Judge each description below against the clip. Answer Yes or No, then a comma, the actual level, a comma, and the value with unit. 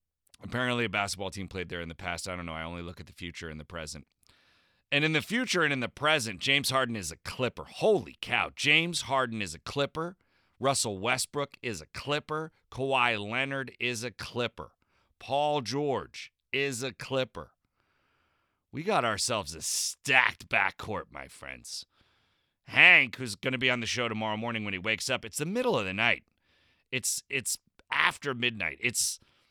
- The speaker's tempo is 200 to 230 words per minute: No, average, 180 wpm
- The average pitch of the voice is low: Yes, low, 125 Hz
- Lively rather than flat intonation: Yes, wide, 5.8 semitones